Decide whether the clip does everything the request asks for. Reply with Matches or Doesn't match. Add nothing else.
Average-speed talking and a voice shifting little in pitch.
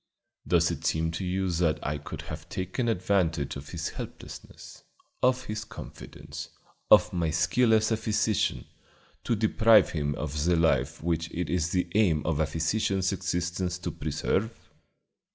Doesn't match